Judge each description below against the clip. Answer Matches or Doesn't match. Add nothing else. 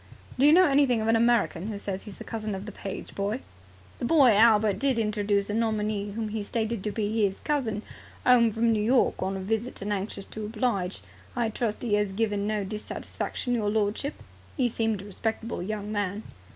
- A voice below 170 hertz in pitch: Doesn't match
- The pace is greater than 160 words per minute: Matches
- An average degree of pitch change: Doesn't match